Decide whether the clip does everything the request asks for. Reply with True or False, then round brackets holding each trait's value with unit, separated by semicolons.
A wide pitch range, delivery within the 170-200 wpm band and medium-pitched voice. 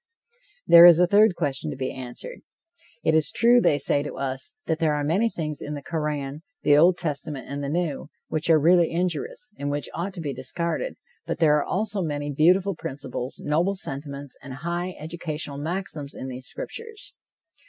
False (3.7 semitones; 185 wpm; 155 Hz)